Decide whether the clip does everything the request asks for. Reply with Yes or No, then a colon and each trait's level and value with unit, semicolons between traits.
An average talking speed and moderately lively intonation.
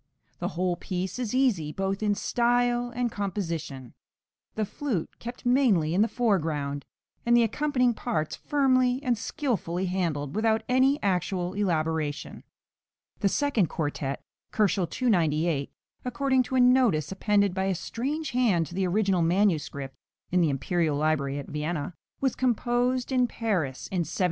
No: average, 145 wpm; wide, 7.0 semitones